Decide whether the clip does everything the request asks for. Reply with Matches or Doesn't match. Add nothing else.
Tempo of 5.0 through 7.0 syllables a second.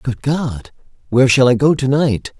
Doesn't match